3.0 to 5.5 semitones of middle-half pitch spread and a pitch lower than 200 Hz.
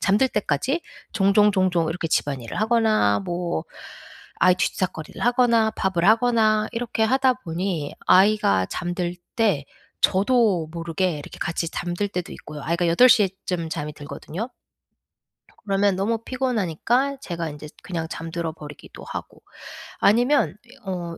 Yes: average, 5.1 semitones; medium, 185 Hz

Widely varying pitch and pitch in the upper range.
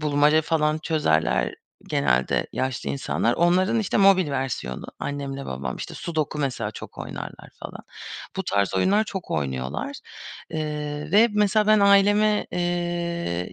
No: wide, 7.6 semitones; medium, 150 Hz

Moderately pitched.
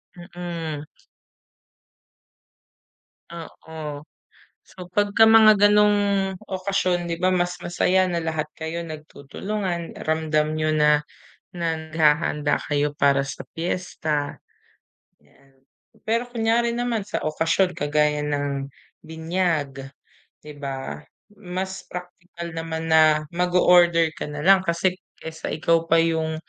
Yes: medium, 165 Hz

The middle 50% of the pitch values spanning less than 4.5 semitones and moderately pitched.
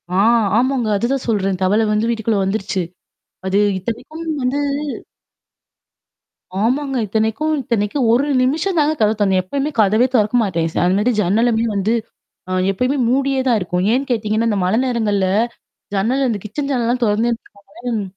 No: average, 3.9 semitones; high, 225 Hz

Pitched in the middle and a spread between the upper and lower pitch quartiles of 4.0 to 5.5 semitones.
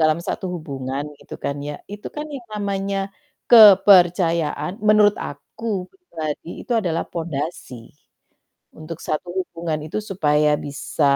Yes: medium, 170 Hz; average, 4.6 semitones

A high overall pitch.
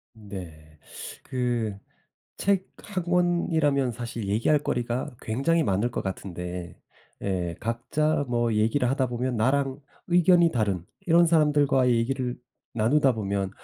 No: low, 125 Hz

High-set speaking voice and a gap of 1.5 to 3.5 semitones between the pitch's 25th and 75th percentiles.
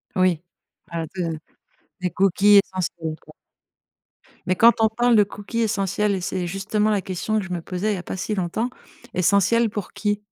Yes: high, 195 Hz; average, 2.8 semitones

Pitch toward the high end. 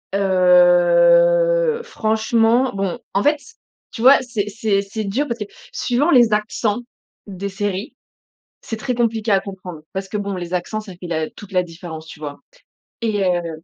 Yes: high, 205 Hz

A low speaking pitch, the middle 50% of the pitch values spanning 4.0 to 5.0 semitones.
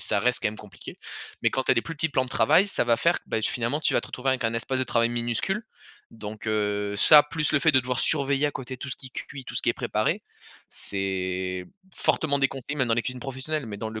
Yes: low, 125 Hz; average, 4.3 semitones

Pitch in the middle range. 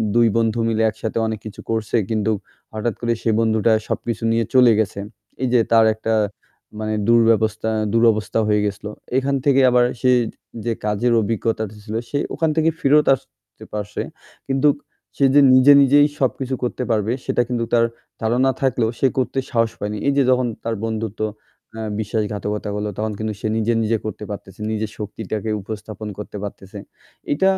No: low, 115 Hz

